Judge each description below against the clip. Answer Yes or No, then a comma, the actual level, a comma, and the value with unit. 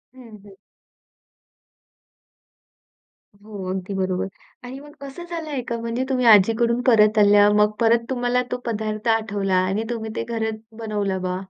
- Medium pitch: No, high, 220 Hz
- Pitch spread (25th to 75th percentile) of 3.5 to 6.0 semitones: No, average, 2.9 semitones